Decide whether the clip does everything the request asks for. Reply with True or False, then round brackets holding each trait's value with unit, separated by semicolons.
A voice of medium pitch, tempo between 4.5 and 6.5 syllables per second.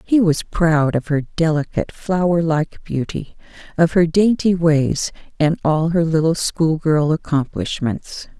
False (160 Hz; 4.1 syllables/s)